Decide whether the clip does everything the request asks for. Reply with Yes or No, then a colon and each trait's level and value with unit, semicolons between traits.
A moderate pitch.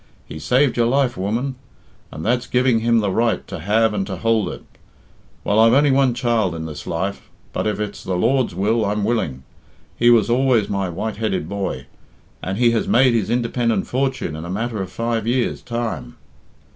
No: low, 115 Hz